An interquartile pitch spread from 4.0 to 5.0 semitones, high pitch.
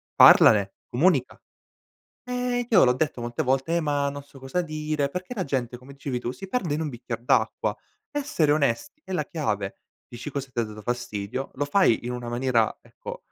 No: average, 4.7 semitones; medium, 140 Hz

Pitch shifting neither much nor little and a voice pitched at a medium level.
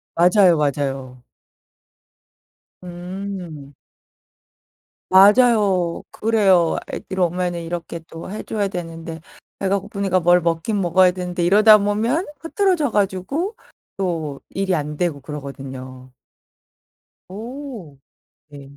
Yes: average, 3.8 semitones; medium, 180 Hz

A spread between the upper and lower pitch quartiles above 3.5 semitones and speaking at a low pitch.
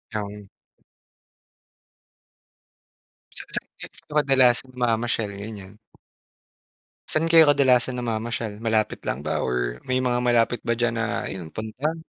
No: average, 3.0 semitones; low, 115 Hz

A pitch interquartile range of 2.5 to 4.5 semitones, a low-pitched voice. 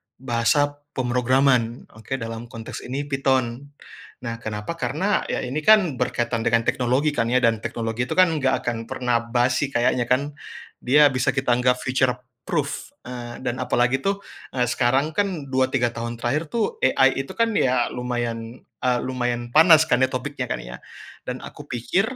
Yes: average, 2.9 semitones; low, 125 Hz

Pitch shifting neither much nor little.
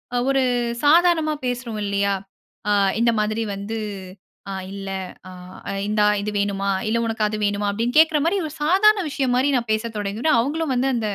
No: wide, 6.0 semitones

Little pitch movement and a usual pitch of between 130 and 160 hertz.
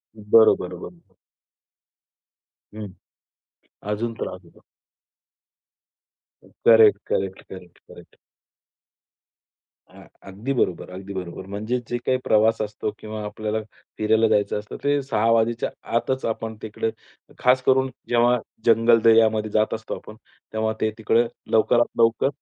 No: narrow, 2.0 semitones; low, 110 Hz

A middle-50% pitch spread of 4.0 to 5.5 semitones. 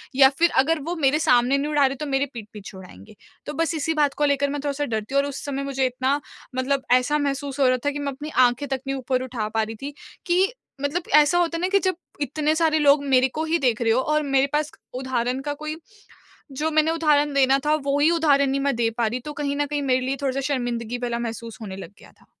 No: average, 2.7 semitones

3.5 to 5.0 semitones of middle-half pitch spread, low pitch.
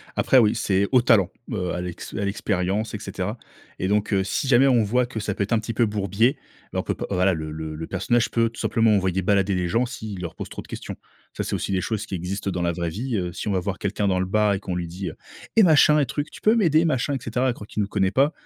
Yes: average, 4.1 semitones; low, 105 Hz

